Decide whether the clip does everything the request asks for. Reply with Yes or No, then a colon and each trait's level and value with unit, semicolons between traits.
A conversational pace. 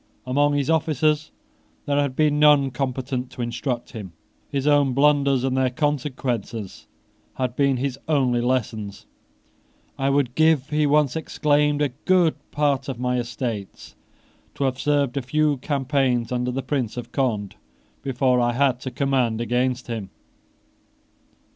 Yes: average, 145 wpm